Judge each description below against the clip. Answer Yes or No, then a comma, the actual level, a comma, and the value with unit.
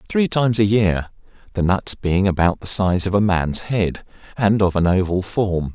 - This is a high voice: No, very low, 95 Hz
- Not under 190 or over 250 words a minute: Yes, average, 200 wpm